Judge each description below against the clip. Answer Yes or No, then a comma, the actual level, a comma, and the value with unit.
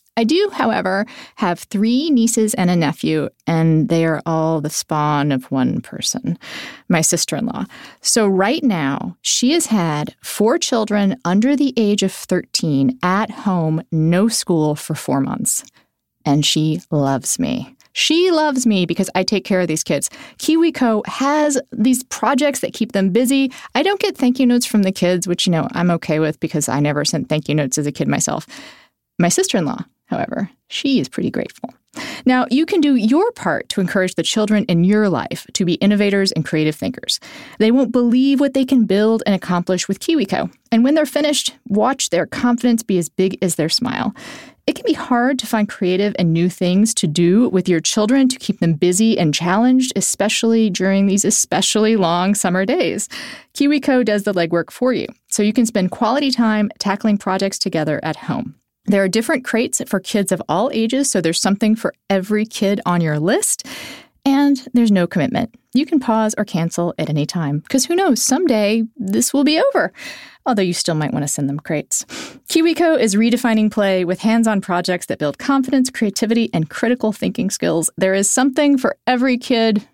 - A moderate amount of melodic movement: No, wide, 6.1 semitones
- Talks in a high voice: Yes, high, 210 Hz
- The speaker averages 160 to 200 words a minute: Yes, average, 190 wpm